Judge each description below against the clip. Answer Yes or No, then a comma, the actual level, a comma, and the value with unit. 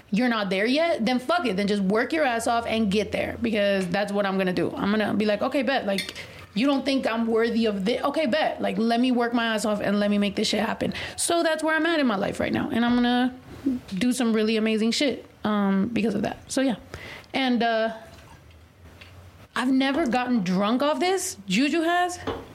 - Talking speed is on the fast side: Yes, fast, 230 wpm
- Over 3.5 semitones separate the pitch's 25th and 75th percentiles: Yes, average, 4.6 semitones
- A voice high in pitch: Yes, high, 230 Hz